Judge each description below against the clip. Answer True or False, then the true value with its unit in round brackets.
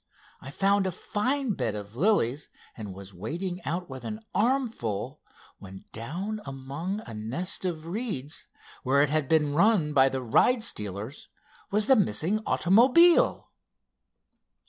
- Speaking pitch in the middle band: True (160 Hz)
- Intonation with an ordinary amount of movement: False (8.4 semitones)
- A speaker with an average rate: True (145 wpm)